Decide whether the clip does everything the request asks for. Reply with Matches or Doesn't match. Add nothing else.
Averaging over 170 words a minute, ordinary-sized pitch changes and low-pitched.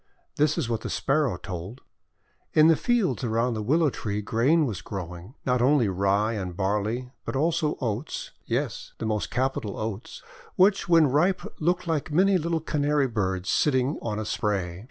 Doesn't match